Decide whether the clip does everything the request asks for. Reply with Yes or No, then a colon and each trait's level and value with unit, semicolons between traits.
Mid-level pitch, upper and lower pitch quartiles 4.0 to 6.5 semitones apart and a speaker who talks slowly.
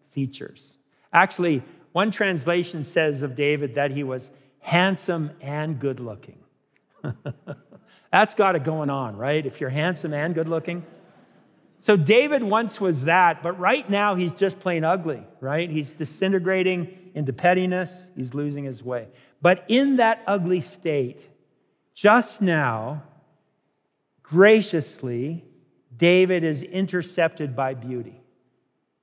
Yes: medium, 165 Hz; average, 4.6 semitones; slow, 125 wpm